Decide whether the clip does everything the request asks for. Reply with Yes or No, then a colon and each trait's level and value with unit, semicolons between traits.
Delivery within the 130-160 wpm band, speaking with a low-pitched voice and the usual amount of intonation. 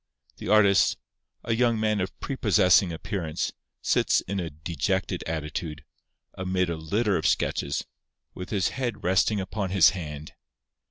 Yes: average, 145 wpm; very low, 95 Hz; average, 4.1 semitones